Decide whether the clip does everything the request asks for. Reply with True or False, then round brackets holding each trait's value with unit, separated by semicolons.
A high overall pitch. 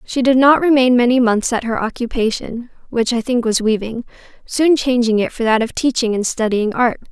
True (240 Hz)